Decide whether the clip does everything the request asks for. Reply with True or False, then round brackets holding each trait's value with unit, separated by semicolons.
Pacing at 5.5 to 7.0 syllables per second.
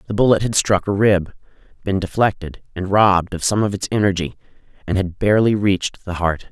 True (5.9 syllables/s)